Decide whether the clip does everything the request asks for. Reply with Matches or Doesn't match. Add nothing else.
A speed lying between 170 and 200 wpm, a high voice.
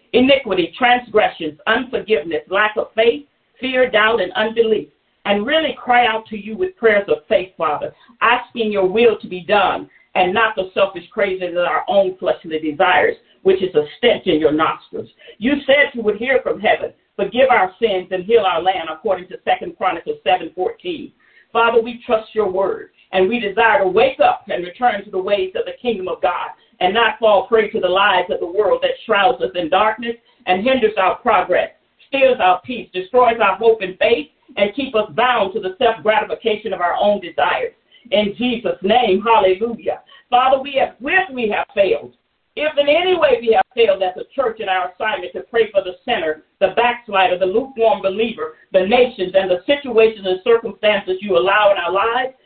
Matches